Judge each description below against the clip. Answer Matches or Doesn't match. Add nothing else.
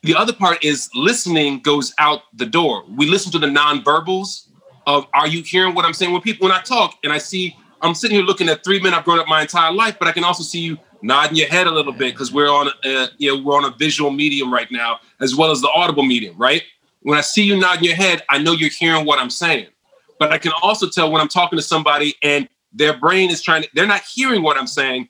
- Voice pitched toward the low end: Doesn't match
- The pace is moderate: Doesn't match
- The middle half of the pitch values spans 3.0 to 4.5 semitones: Matches